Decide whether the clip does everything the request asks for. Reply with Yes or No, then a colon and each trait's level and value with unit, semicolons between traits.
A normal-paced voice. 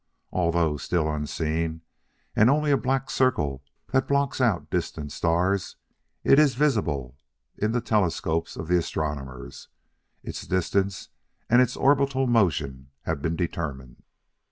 No: slow, 130 wpm